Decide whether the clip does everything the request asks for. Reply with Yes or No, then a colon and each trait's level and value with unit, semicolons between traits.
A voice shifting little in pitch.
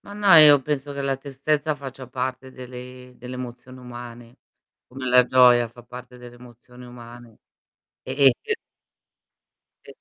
Yes: narrow, 1.7 semitones